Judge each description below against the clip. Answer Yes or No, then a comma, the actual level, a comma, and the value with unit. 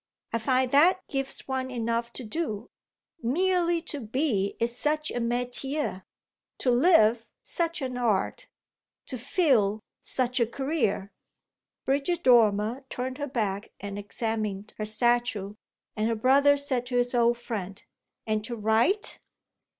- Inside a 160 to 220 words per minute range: No, slow, 135 wpm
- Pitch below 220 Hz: No, high, 245 Hz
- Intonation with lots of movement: No, average, 4.1 semitones